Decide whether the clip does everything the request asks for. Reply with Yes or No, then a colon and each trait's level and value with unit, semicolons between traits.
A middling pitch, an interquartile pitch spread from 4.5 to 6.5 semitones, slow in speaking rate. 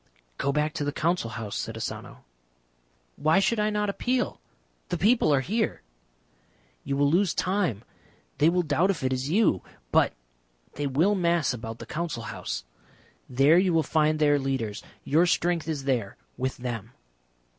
No: medium, 150 Hz; average, 5.2 semitones; average, 165 wpm